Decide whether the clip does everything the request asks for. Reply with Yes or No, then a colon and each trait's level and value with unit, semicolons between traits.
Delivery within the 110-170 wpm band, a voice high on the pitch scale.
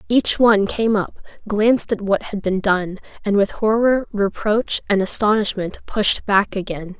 Yes: average, 165 wpm; high, 205 Hz